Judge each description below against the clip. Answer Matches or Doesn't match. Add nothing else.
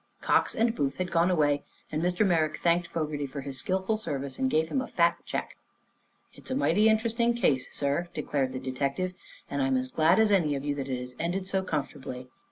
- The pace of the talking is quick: Matches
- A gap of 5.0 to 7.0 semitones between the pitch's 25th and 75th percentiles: Matches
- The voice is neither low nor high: Matches